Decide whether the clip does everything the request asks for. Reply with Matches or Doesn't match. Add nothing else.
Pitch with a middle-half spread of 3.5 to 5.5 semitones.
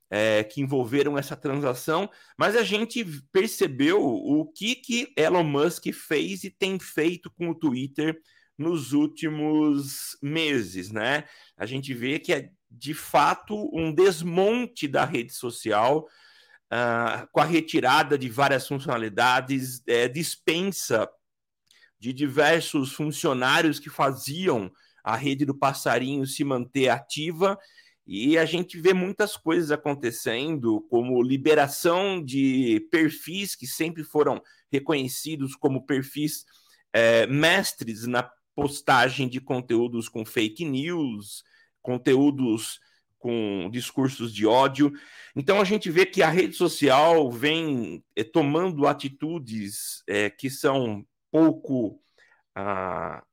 Matches